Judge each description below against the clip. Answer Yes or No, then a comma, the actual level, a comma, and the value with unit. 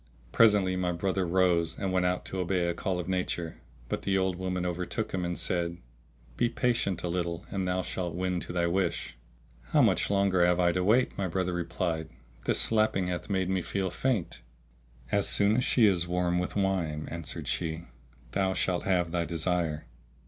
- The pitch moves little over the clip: Yes, narrow, 1.8 semitones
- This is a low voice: Yes, very low, 90 Hz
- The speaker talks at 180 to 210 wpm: Yes, average, 190 wpm